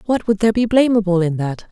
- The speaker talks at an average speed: No, fast, 245 wpm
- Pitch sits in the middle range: No, high, 205 Hz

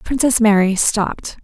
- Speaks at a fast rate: No, slow, 125 wpm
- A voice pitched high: Yes, high, 215 Hz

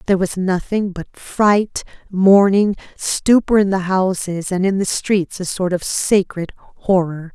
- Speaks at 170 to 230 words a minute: No, average, 155 wpm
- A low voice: No, high, 190 Hz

